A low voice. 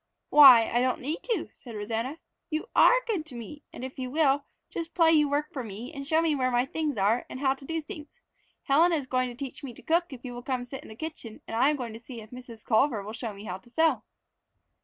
No: very high, 265 Hz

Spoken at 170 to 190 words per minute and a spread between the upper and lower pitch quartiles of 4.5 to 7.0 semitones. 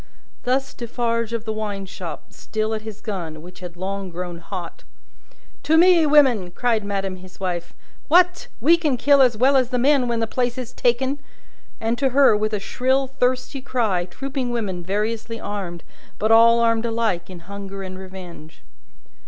Yes: average, 175 wpm; average, 5.0 semitones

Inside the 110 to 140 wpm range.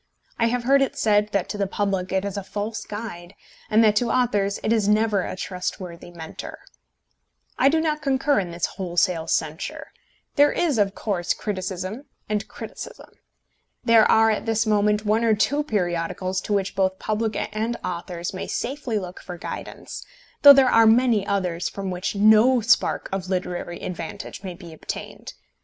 No: average, 175 wpm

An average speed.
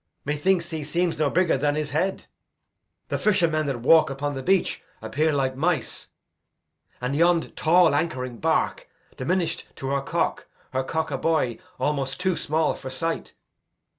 Yes: average, 155 wpm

